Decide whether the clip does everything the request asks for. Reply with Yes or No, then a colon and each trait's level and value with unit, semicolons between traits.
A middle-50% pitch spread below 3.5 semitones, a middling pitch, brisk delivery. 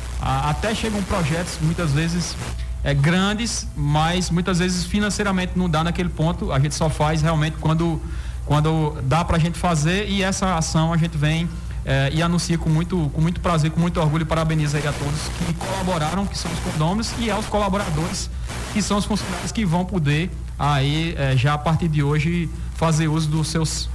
Yes: average, 2.8 semitones; medium, 160 Hz; fast, 190 wpm